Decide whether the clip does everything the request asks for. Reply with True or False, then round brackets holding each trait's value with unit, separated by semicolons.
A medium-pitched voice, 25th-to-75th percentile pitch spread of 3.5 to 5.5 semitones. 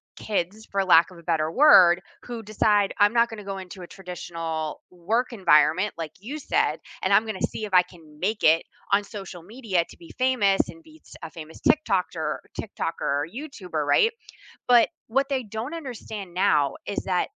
False (195 Hz; 4.8 semitones)